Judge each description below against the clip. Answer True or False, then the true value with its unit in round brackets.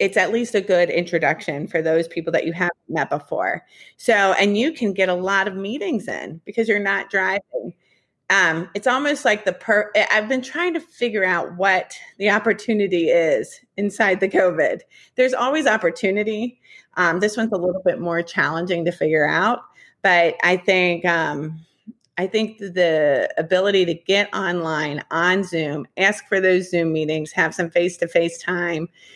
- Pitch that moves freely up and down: False (3.8 semitones)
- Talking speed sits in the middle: True (175 wpm)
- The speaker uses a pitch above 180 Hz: True (190 Hz)